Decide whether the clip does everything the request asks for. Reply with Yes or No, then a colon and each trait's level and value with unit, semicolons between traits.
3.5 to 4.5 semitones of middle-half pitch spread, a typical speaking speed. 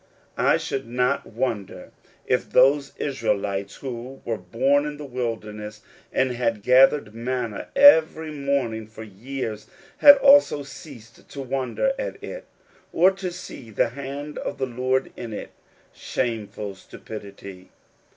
No: average, 4.2 semitones; slow, 130 wpm